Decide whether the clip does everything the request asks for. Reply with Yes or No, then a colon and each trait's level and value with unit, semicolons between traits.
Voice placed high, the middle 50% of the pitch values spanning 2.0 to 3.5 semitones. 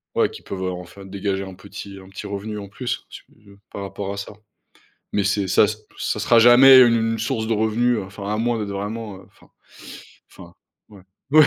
No: low, 105 Hz; narrow, 2.5 semitones